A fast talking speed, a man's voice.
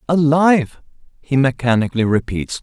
No: slow, 90 wpm; male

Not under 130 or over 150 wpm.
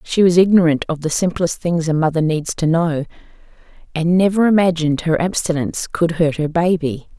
No: average, 175 wpm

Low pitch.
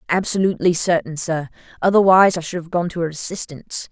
No: medium, 170 Hz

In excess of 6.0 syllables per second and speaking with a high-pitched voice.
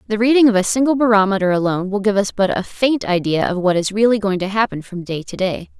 Yes: 6.3 syllables/s; high, 205 Hz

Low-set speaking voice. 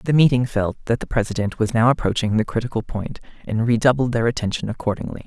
Yes: low, 115 Hz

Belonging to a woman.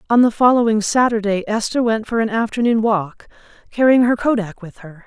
Yes: female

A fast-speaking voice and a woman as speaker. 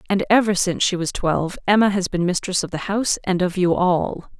Yes: fast, 230 wpm; female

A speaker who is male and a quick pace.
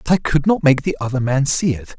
Yes: male; fast, 300 wpm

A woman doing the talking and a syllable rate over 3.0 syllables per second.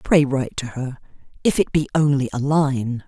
Yes: female; 5.0 syllables/s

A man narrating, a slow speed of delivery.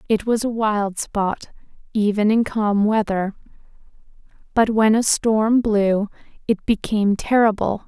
No: female; slow, 130 wpm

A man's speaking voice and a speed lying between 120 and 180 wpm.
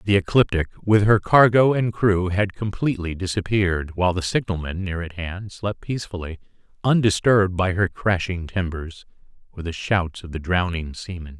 Yes: male; average, 160 wpm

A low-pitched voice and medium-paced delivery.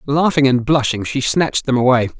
Yes: low, 130 Hz; average, 190 wpm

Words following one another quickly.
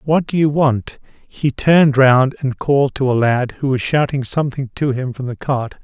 Yes: fast, 215 wpm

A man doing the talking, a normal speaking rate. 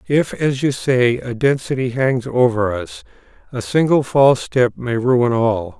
Yes: male; average, 165 wpm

